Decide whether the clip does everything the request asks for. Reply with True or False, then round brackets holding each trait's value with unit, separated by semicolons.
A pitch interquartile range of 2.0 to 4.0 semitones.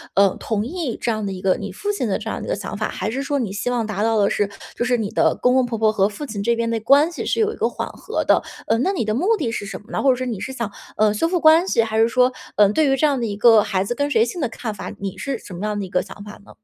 False (4.5 semitones)